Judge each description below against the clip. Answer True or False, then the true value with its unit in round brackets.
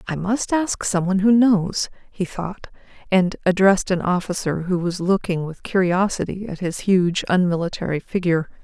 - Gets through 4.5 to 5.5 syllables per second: True (5.0 syllables/s)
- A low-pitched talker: False (185 Hz)